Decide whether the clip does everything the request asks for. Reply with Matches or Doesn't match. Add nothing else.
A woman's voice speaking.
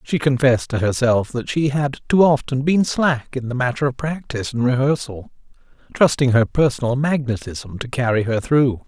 Doesn't match